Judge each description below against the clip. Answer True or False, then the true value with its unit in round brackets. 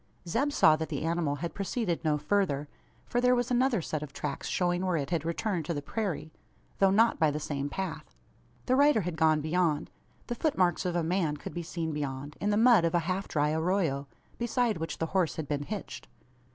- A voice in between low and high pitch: True (170 Hz)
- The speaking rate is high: True (220 wpm)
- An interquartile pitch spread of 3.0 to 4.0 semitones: False (4.8 semitones)